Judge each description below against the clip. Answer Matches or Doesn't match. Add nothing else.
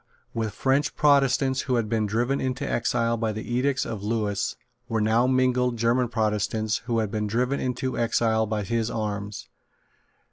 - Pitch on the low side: Matches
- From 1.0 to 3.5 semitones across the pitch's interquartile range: Matches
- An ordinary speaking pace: Matches